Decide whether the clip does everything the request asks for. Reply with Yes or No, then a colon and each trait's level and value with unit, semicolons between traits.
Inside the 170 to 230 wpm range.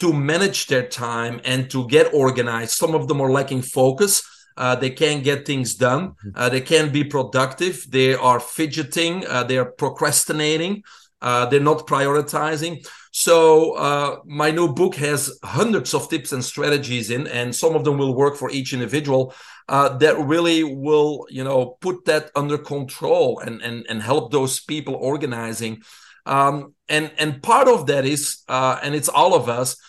Yes: average, 175 wpm